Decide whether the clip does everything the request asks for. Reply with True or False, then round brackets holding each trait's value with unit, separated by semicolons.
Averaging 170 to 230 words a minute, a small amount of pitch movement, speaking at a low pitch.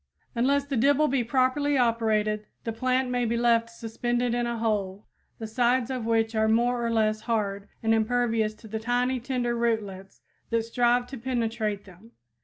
False (175 wpm; 2.0 semitones; 230 Hz)